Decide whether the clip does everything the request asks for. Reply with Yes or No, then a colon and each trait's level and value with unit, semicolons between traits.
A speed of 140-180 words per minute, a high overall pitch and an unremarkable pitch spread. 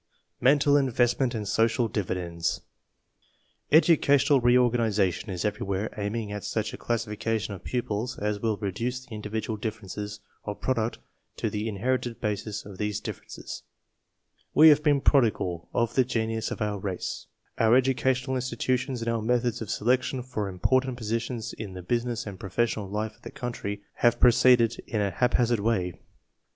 No: average, 155 wpm; low, 115 Hz; average, 3.2 semitones